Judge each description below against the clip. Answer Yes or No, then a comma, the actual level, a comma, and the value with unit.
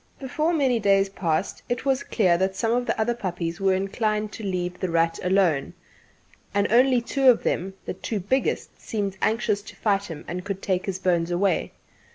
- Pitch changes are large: No, average, 4.1 semitones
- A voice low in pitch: No, high, 195 Hz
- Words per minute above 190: Yes, average, 200 wpm